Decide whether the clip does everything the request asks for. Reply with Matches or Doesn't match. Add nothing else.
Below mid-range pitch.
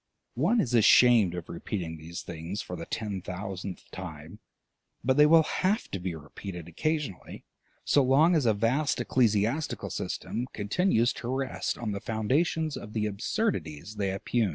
Matches